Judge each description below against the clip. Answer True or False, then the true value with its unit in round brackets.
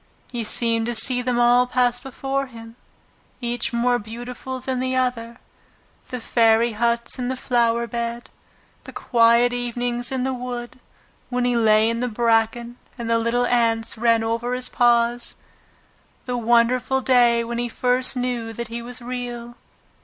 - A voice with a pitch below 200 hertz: False (240 Hz)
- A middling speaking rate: True (160 wpm)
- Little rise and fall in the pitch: True (1.1 semitones)